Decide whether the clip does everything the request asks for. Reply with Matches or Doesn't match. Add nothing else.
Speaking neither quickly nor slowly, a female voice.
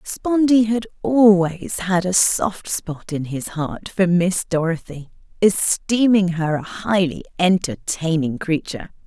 Doesn't match